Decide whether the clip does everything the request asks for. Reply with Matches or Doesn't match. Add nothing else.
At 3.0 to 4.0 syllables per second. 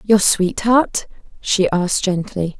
Matches